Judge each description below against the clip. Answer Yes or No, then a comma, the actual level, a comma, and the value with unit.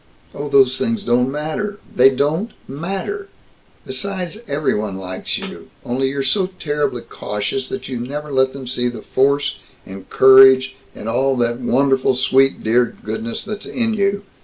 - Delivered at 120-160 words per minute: Yes, average, 155 wpm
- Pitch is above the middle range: No, low, 135 Hz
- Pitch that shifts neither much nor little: Yes, average, 4.1 semitones